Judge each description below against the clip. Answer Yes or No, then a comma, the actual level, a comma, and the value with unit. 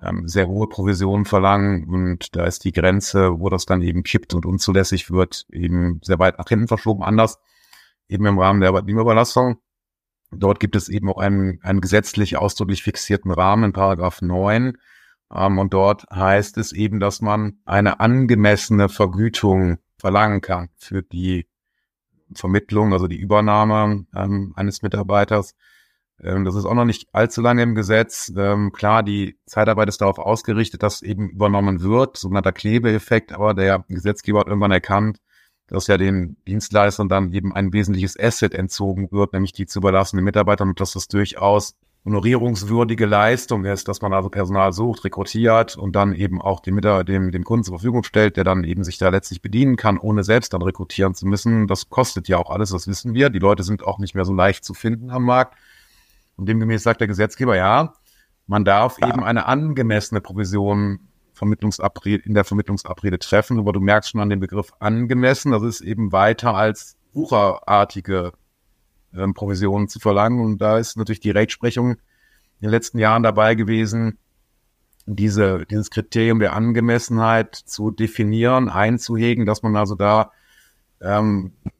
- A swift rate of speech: No, average, 165 wpm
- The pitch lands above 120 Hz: No, low, 100 Hz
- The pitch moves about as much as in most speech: No, narrow, 2.2 semitones